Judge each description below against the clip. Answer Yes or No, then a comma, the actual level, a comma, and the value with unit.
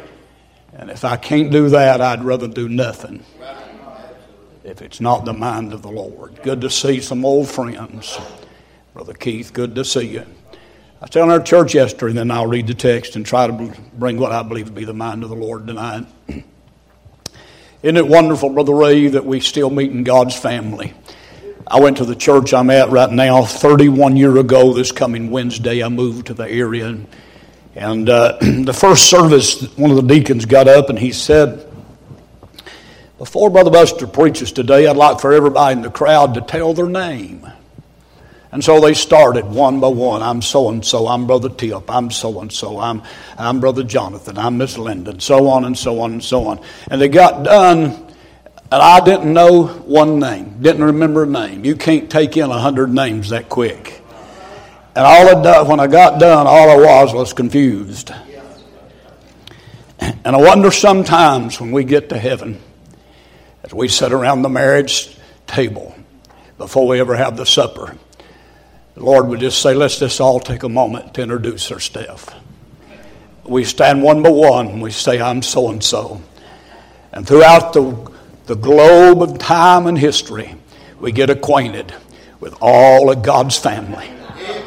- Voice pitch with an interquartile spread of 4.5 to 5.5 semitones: No, average, 3.5 semitones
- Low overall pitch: Yes, low, 130 Hz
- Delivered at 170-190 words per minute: Yes, average, 180 wpm